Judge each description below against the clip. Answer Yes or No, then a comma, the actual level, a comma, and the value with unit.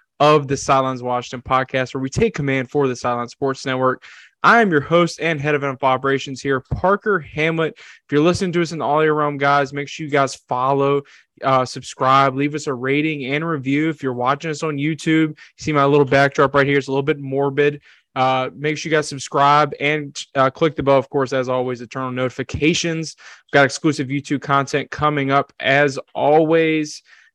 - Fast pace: Yes, fast, 210 wpm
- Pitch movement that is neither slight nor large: No, narrow, 2.3 semitones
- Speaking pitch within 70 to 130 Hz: No, medium, 140 Hz